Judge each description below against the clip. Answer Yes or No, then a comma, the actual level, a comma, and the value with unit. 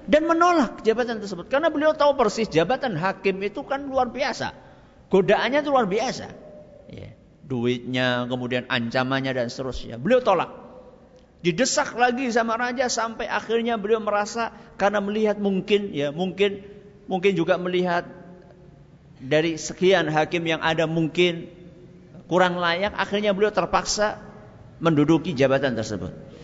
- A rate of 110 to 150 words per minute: Yes, average, 125 wpm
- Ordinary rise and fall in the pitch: No, wide, 6.0 semitones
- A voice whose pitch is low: No, high, 190 Hz